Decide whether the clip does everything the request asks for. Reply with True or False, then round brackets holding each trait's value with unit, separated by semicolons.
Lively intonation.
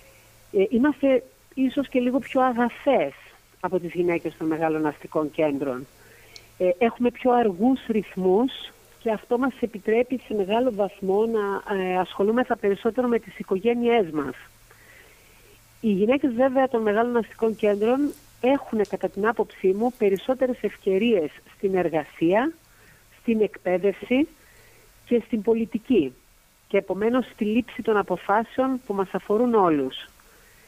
False (4.5 semitones)